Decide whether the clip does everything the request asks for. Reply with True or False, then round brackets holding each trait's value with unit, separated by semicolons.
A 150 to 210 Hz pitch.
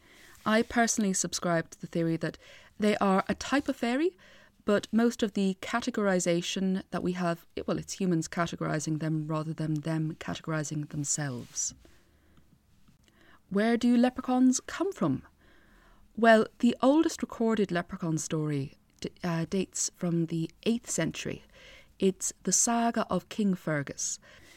True (185 Hz)